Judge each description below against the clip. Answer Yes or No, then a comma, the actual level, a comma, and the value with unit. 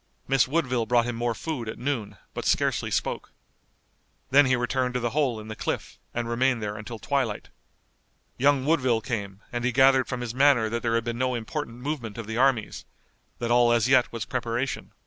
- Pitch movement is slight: Yes, narrow, 2.3 semitones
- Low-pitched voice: Yes, low, 120 Hz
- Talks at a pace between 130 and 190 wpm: No, average, 200 wpm